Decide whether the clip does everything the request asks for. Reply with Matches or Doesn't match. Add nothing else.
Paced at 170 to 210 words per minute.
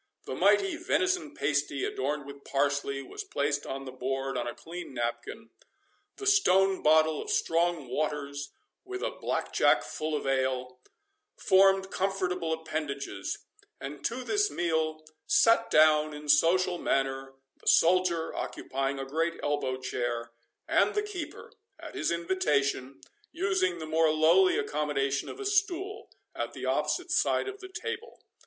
Doesn't match